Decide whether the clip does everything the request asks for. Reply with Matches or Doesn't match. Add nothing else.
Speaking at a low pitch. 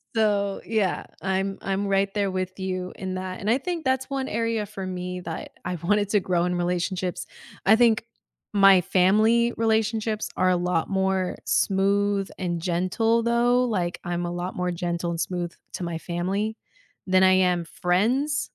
Doesn't match